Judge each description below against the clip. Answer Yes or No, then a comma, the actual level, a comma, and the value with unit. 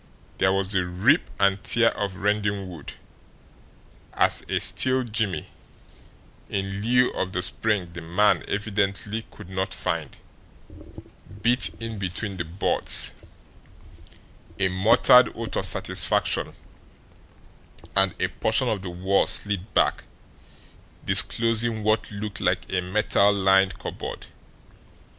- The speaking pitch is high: No, low, 100 Hz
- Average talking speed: No, slow, 120 wpm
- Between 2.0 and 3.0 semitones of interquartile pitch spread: Yes, narrow, 2.6 semitones